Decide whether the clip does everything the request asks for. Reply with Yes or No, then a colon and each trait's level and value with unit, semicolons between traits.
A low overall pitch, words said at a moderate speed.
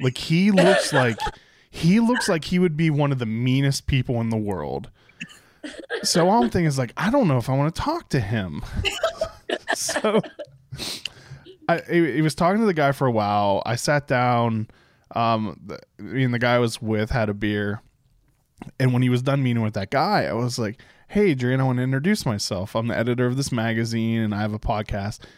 No: low, 130 Hz; fast, 210 wpm